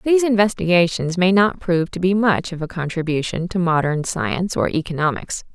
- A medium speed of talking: Yes, average, 175 wpm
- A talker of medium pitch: Yes, medium, 180 Hz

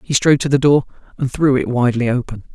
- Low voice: Yes, low, 130 Hz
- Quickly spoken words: Yes, fast, 210 wpm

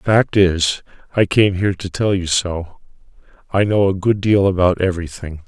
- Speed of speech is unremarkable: Yes, average, 165 wpm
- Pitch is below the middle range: Yes, very low, 95 Hz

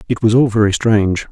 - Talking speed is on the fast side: Yes, fast, 230 wpm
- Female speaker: No, male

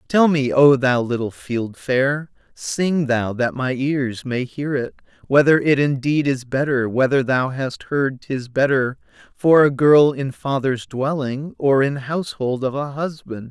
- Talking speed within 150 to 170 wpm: Yes, average, 165 wpm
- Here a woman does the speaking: No, male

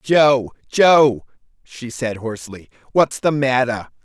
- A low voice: Yes, low, 125 Hz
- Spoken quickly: No, slow, 135 wpm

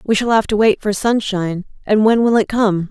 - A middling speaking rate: No, fast, 250 wpm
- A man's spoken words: No, female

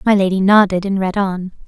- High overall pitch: Yes, high, 195 Hz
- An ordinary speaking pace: No, fast, 215 wpm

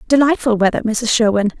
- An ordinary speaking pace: Yes, average, 150 wpm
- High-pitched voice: Yes, high, 230 Hz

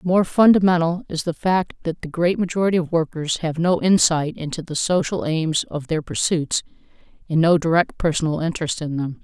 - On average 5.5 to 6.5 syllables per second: No, 5.3 syllables/s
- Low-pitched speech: No, medium, 165 Hz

